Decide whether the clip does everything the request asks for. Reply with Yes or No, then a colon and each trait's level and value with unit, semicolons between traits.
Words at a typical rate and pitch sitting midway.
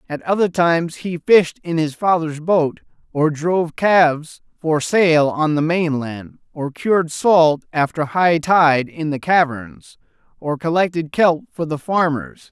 Yes: average, 155 wpm; medium, 160 Hz